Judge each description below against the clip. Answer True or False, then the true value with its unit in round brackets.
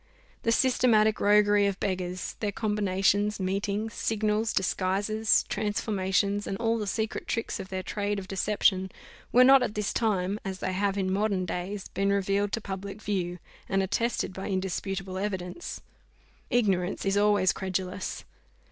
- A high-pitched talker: True (200 Hz)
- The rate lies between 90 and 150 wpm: True (145 wpm)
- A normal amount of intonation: False (1.9 semitones)